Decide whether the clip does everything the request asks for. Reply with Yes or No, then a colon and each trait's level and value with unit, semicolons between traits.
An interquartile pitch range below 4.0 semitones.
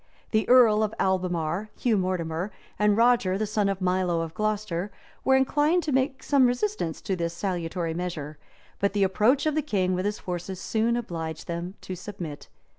No: average, 4.3 semitones